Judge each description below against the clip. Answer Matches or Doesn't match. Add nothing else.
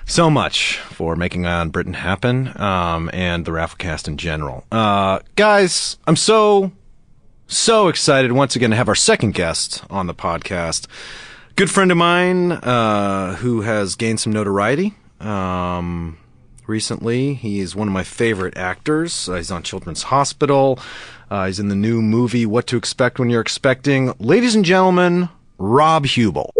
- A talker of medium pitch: Doesn't match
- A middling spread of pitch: Doesn't match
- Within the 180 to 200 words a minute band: Doesn't match